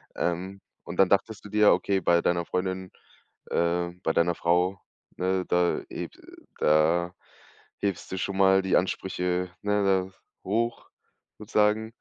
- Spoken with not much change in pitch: Yes, narrow, 2.0 semitones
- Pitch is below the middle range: Yes, very low, 95 Hz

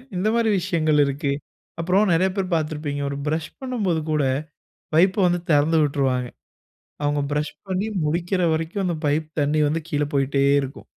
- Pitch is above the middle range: No, medium, 160 Hz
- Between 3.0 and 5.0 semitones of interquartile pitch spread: Yes, average, 3.8 semitones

